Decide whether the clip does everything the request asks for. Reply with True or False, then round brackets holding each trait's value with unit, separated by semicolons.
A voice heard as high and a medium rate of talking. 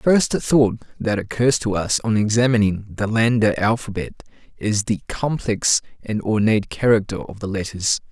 False (110 Hz; 155 wpm)